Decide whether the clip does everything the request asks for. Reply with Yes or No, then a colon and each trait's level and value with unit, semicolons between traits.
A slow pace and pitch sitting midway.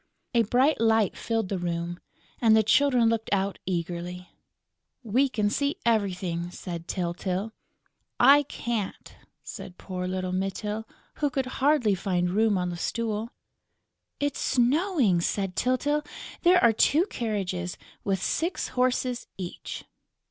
No: slow, 130 wpm; high, 215 Hz